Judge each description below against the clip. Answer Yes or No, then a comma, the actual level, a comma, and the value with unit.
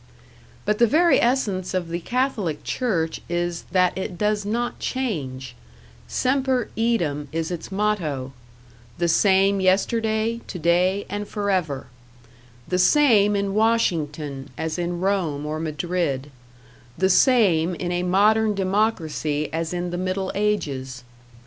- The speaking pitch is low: No, medium, 185 Hz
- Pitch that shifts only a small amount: No, average, 4.6 semitones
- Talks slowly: Yes, slow, 125 wpm